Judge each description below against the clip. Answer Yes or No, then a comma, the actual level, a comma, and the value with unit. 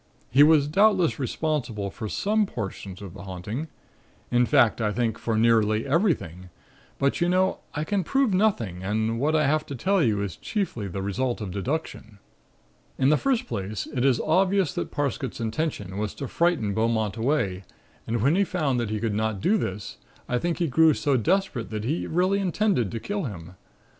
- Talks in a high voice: No, low, 125 Hz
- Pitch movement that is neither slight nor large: No, wide, 7.7 semitones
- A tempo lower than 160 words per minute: No, average, 190 wpm